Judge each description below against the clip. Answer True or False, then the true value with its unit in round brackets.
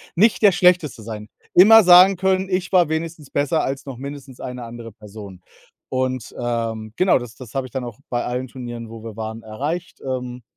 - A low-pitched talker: True (130 Hz)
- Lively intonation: True (6.5 semitones)